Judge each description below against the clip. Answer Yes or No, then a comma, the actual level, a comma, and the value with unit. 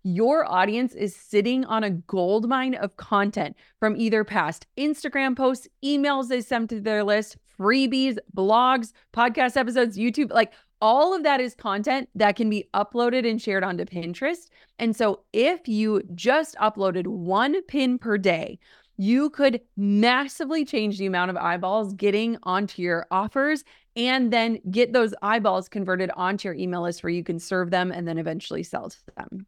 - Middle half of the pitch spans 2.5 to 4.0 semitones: No, average, 4.8 semitones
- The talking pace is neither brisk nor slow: Yes, average, 165 wpm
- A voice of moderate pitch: No, high, 220 Hz